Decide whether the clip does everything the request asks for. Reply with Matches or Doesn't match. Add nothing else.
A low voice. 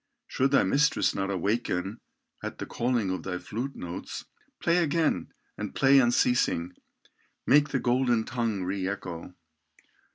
Matches